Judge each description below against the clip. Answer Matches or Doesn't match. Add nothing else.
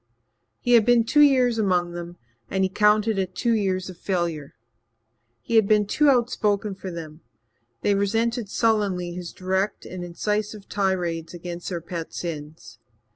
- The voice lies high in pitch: Matches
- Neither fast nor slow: Matches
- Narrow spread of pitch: Doesn't match